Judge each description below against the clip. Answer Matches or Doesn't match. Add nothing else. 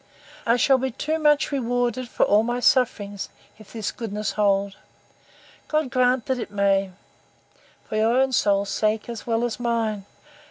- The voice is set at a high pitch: Matches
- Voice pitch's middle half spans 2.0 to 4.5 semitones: Matches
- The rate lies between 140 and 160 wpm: Matches